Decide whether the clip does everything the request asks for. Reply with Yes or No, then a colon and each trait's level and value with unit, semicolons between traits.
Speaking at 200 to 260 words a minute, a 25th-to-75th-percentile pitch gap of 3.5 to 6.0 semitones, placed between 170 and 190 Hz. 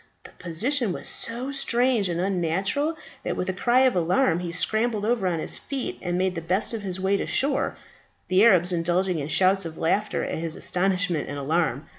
Yes: fast, 205 wpm; average, 5.1 semitones; medium, 185 Hz